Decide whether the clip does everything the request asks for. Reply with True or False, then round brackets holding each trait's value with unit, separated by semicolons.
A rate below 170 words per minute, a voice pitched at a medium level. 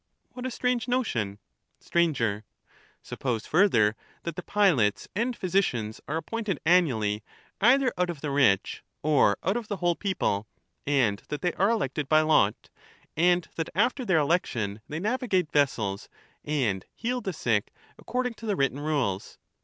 True (155 wpm; 160 Hz)